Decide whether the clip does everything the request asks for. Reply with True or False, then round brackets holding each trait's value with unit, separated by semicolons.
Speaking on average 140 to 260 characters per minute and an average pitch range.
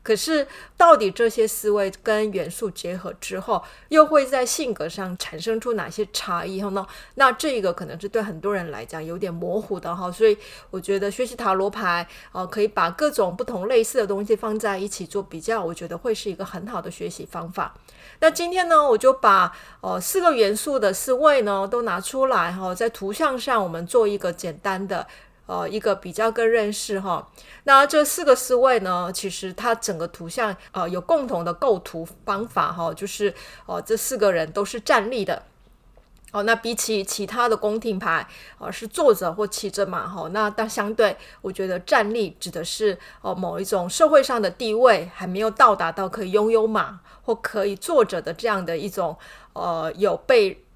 False (285 characters per minute; 4.0 semitones)